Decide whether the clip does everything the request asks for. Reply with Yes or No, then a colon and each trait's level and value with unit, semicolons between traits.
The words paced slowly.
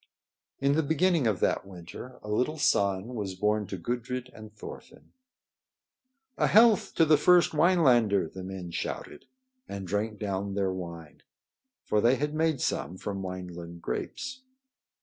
No: average, 150 wpm